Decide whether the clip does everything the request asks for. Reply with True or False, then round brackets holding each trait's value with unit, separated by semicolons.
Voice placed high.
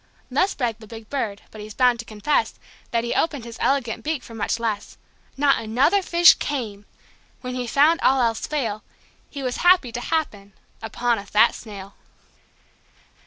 True (240 Hz)